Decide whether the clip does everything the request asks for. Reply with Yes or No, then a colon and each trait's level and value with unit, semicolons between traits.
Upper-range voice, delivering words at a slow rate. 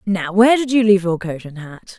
No: high, 195 Hz; fast, 270 wpm